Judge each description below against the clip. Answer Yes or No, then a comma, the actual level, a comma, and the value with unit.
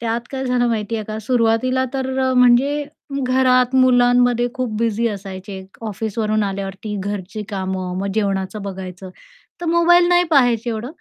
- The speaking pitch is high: Yes, high, 230 Hz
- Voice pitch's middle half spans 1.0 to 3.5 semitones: No, average, 4.1 semitones